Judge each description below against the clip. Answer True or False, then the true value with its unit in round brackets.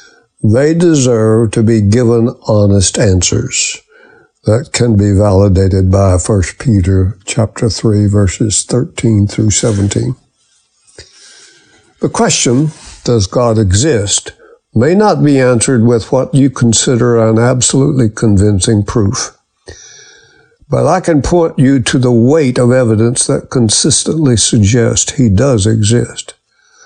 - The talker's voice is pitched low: True (120 Hz)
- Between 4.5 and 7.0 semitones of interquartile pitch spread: True (5.0 semitones)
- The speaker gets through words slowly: True (120 wpm)